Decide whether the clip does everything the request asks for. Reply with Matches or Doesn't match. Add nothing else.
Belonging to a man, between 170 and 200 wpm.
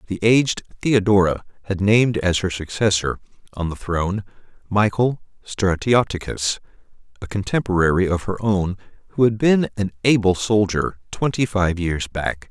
Doesn't match